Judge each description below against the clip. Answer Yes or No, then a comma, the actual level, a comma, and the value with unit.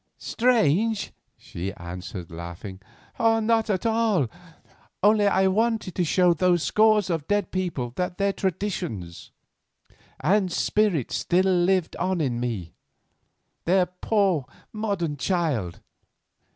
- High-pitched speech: No, medium, 180 Hz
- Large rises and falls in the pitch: Yes, wide, 6.7 semitones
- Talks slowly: Yes, slow, 110 wpm